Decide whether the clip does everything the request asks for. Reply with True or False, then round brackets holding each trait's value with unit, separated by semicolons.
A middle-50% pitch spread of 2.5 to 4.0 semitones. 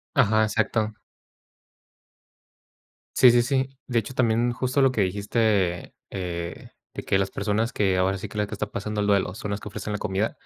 True (2.9 semitones)